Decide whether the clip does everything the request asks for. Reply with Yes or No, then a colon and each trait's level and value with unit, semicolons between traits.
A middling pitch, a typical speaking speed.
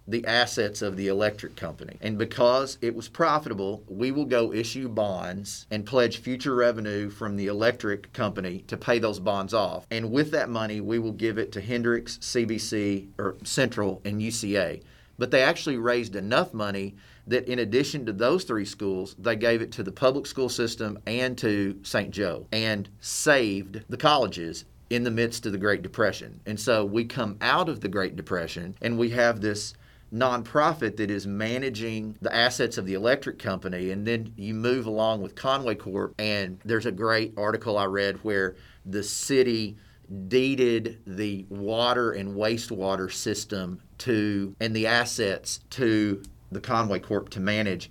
No: low, 110 Hz; average, 170 wpm